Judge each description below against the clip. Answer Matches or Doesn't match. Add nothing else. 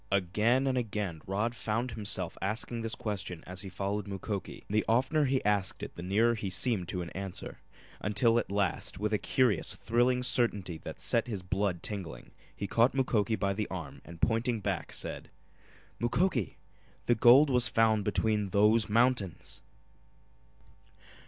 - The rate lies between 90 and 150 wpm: Doesn't match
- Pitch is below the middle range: Matches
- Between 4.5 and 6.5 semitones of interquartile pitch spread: Doesn't match